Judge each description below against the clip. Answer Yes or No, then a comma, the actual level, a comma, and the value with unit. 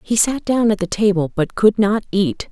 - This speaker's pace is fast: Yes, fast, 240 wpm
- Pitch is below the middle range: No, high, 205 Hz